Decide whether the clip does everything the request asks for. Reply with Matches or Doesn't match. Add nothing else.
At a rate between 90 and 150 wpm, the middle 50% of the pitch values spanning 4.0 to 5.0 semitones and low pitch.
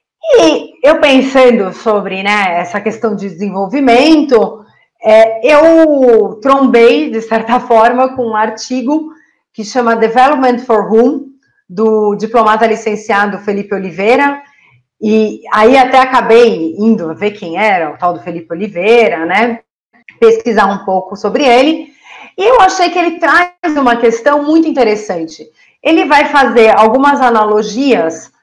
Doesn't match